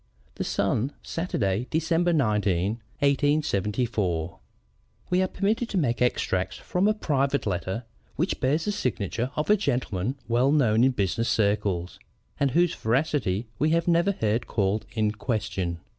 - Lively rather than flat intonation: Yes, wide, 7.0 semitones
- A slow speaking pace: No, average, 145 wpm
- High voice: No, low, 120 Hz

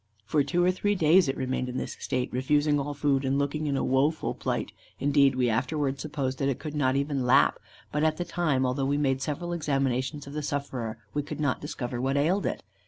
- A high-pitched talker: No, medium, 140 Hz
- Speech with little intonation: Yes, narrow, 2.3 semitones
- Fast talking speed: Yes, fast, 225 wpm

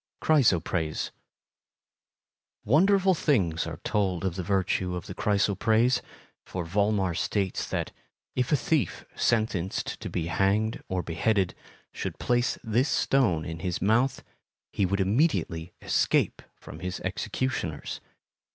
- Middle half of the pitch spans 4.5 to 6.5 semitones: Yes, wide, 5.4 semitones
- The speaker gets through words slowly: Yes, slow, 125 wpm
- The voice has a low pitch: Yes, low, 100 Hz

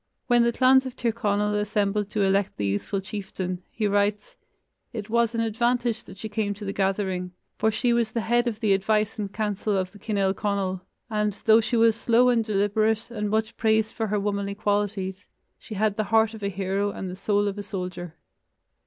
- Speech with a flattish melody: Yes, narrow, 2.0 semitones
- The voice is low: No, high, 210 Hz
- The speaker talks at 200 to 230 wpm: Yes, fast, 205 wpm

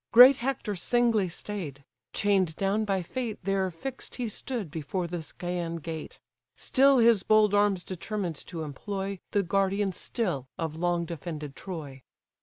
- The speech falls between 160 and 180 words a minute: No, average, 145 wpm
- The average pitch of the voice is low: No, high, 190 Hz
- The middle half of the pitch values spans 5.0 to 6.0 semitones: No, average, 4.1 semitones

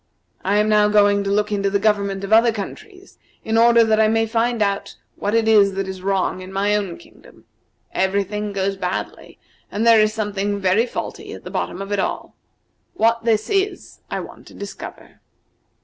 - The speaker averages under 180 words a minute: No, average, 195 wpm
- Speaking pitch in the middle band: No, high, 210 Hz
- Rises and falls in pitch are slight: Yes, narrow, 2.1 semitones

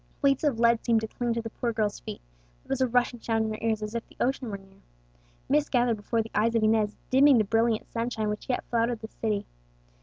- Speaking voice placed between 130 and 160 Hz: No, high, 230 Hz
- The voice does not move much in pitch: Yes, narrow, 1.9 semitones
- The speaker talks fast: Yes, fast, 245 wpm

